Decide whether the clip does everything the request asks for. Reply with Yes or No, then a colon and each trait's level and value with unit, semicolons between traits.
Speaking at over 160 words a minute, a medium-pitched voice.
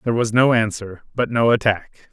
No: average, 200 wpm; low, 115 Hz